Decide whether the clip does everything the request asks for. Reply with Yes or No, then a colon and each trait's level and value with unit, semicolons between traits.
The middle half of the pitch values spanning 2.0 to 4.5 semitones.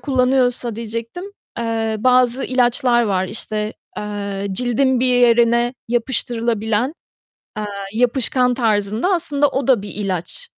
Yes: average, 2.8 semitones